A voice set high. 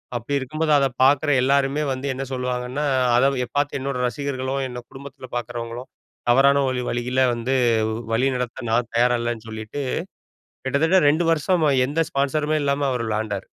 No: low, 130 Hz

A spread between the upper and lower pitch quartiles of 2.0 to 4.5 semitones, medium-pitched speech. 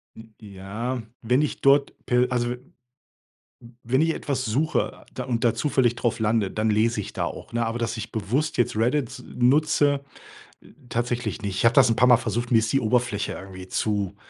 No: average, 2.7 semitones; low, 120 Hz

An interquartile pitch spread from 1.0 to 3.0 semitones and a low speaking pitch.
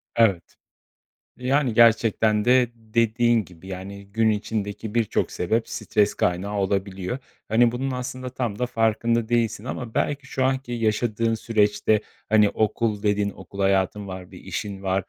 Yes: average, 2.7 semitones; low, 110 Hz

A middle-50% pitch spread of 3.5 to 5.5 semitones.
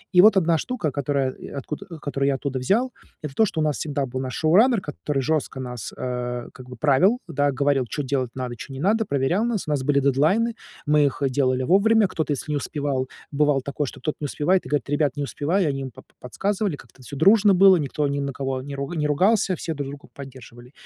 Yes: average, 4.5 semitones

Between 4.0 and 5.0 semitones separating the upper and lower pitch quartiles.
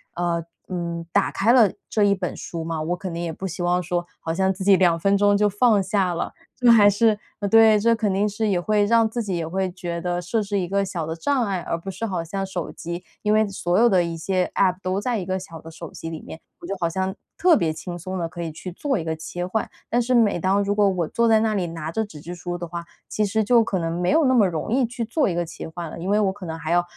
No: average, 3.5 semitones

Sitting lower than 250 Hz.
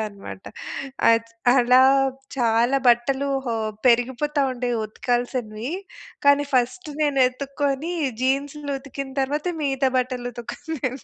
No: very high, 260 Hz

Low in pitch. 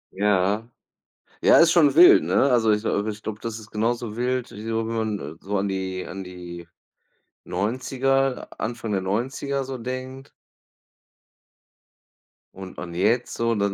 Yes: low, 110 Hz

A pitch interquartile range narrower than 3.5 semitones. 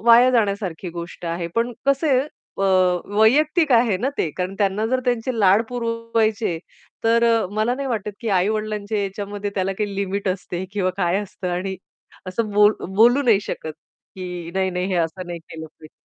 No: average, 3.8 semitones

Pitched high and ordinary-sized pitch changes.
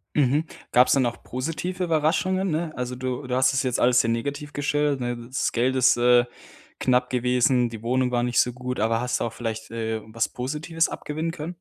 No: low, 125 Hz; average, 3.4 semitones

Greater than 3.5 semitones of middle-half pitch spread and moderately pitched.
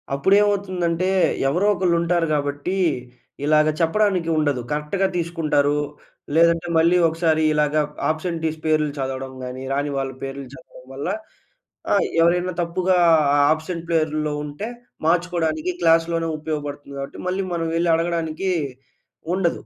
No: average, 2.7 semitones; medium, 165 Hz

